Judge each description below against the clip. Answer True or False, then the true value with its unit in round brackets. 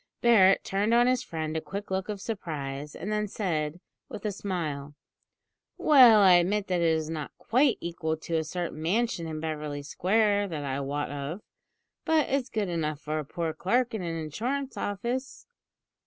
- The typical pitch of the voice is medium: True (180 Hz)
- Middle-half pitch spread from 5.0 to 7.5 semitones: True (5.4 semitones)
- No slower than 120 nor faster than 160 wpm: False (180 wpm)